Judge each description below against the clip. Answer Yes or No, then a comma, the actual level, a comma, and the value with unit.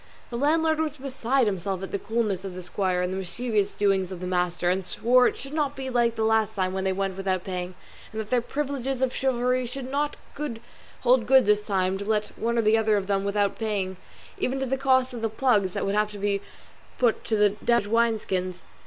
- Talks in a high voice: Yes, high, 215 Hz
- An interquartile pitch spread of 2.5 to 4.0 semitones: No, average, 4.6 semitones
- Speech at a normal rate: No, fast, 230 wpm